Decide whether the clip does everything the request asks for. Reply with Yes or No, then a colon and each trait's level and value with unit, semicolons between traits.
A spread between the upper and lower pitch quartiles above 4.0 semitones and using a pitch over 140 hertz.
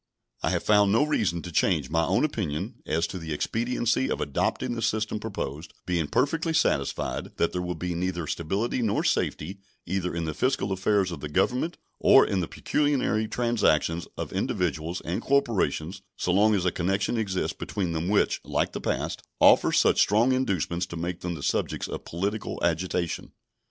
No: average, 4.6 semitones; very low, 95 Hz